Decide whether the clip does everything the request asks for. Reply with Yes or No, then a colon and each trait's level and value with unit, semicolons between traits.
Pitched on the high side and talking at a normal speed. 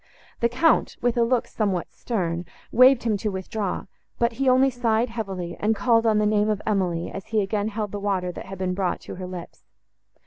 No: high, 210 Hz; fast, 210 wpm